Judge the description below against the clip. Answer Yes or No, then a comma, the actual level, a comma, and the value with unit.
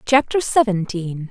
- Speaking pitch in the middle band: No, high, 215 Hz